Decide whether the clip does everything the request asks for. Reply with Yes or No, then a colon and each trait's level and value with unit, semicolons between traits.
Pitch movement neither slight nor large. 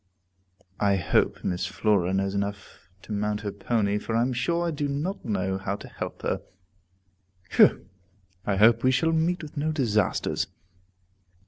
No: wide, 6.1 semitones